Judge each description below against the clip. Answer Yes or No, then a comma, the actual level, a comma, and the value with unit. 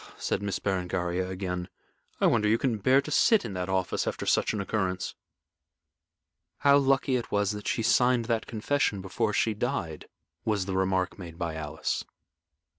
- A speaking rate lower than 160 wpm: No, average, 170 wpm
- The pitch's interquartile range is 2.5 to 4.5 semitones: Yes, average, 4.1 semitones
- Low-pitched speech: Yes, low, 100 Hz